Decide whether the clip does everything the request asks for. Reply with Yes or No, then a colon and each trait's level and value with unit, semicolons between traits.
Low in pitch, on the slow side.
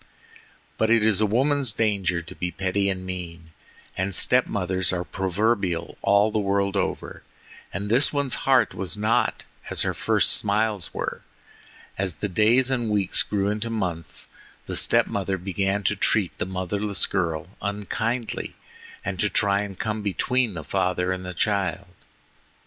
No: low, 100 Hz; average, 155 wpm